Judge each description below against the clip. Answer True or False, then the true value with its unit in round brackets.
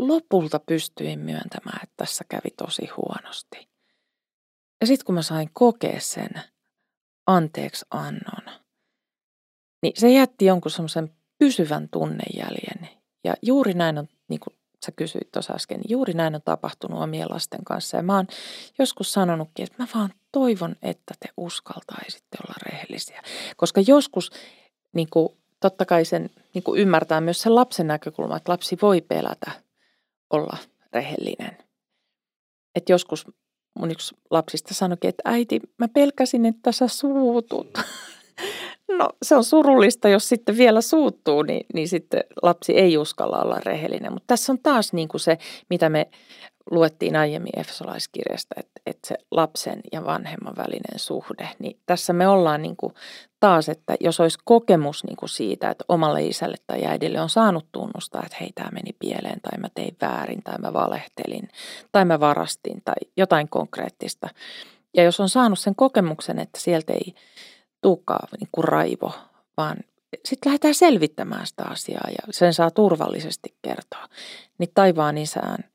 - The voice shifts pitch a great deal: True (6.5 semitones)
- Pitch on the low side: False (185 Hz)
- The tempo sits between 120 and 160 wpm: True (150 wpm)